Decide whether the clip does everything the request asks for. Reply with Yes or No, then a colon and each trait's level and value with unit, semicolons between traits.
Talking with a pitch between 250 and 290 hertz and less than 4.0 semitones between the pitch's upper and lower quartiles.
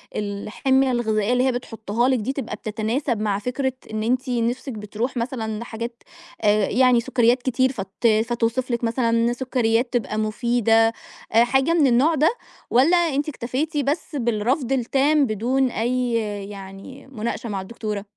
No: high, 240 Hz; average, 2.9 semitones